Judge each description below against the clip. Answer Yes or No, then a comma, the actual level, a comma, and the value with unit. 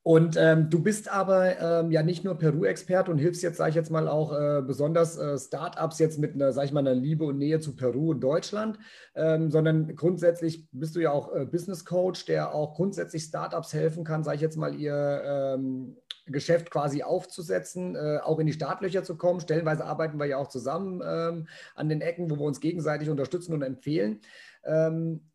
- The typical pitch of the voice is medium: Yes, medium, 160 Hz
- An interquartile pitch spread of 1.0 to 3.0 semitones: Yes, narrow, 2.4 semitones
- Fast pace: Yes, fast, 205 wpm